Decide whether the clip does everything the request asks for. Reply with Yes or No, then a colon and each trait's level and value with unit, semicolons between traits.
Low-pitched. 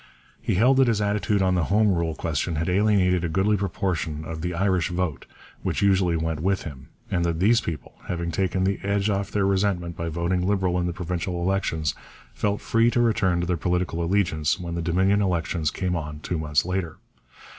Yes: very low, 90 Hz